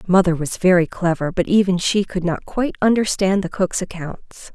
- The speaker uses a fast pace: No, average, 185 wpm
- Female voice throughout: Yes, female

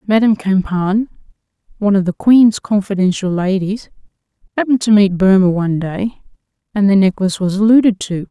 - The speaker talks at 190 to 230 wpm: No, average, 145 wpm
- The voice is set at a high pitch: Yes, high, 200 Hz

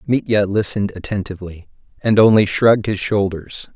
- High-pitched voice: No, low, 100 Hz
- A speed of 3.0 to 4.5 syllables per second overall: No, 5.5 syllables/s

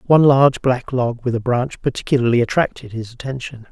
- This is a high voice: No, low, 125 Hz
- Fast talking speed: No, average, 180 wpm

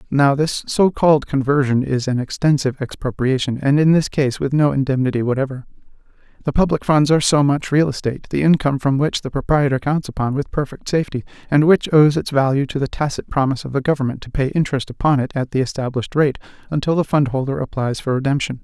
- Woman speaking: No, male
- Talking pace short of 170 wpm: No, fast, 205 wpm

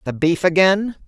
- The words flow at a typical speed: Yes, average, 165 wpm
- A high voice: No, medium, 175 Hz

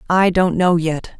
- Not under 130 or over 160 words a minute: No, average, 200 wpm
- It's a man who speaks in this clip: No, female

